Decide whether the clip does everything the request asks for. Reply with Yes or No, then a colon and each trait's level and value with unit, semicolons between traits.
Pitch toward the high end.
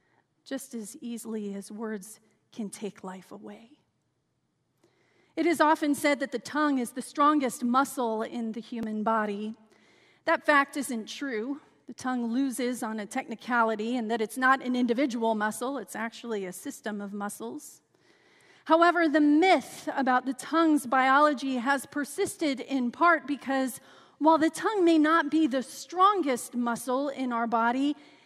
Yes: very high, 260 Hz